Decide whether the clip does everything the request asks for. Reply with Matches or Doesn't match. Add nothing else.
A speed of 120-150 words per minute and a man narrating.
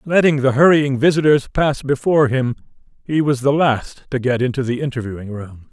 Doesn't match